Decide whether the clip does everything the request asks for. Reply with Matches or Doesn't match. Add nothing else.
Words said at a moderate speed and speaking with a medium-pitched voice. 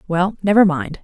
Matches